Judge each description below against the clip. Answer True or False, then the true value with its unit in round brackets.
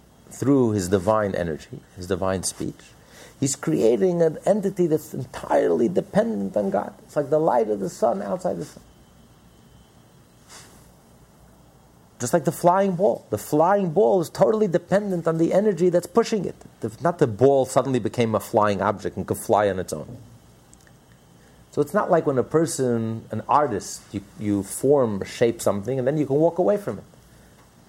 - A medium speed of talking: True (170 wpm)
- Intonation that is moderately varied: False (8.8 semitones)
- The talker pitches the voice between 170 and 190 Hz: False (140 Hz)